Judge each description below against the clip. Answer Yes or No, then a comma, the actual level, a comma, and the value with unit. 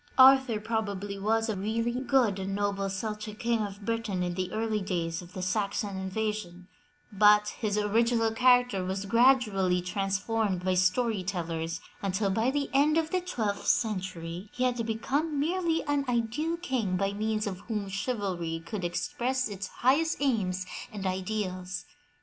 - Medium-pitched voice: No, high, 210 Hz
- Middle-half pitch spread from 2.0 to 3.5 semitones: No, average, 3.9 semitones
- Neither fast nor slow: Yes, average, 155 wpm